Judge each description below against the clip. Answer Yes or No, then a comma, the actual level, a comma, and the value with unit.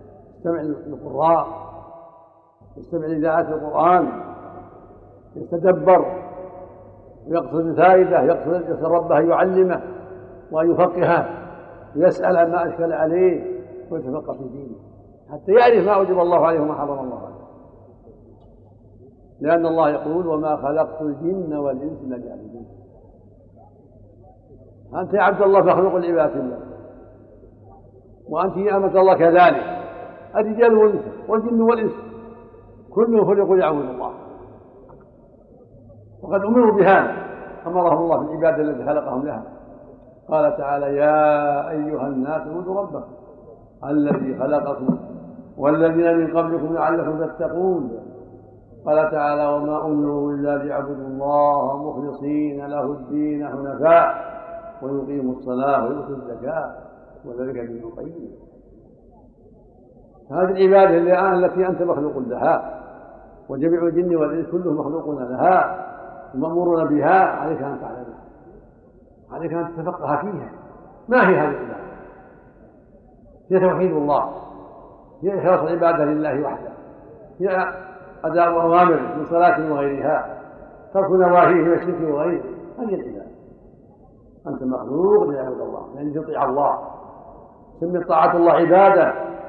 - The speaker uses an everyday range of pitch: Yes, average, 4.2 semitones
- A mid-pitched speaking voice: Yes, medium, 160 Hz